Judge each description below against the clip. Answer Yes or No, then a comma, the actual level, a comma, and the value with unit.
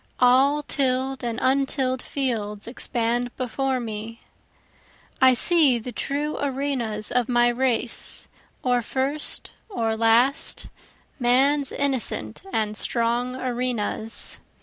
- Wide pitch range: No, narrow, 2.5 semitones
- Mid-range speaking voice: No, very high, 250 Hz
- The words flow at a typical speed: No, slow, 105 wpm